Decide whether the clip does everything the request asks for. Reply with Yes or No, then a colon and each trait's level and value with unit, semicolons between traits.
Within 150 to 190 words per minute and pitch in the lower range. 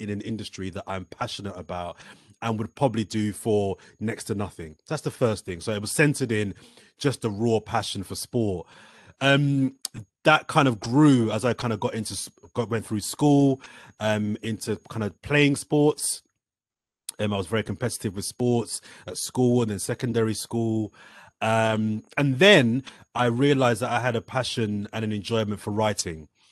Yes: average, 180 wpm; low, 110 Hz